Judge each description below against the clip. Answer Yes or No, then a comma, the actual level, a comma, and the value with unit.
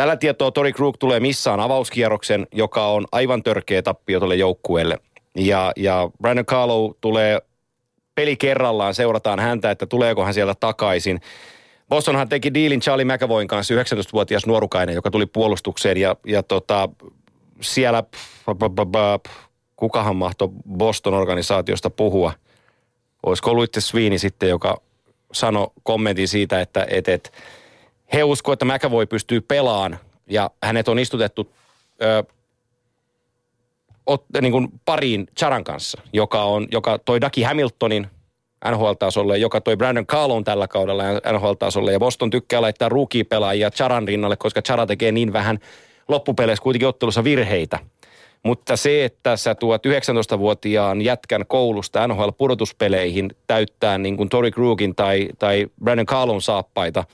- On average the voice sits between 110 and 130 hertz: Yes, low, 115 Hz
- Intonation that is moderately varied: Yes, average, 3.3 semitones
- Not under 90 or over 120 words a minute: No, average, 130 wpm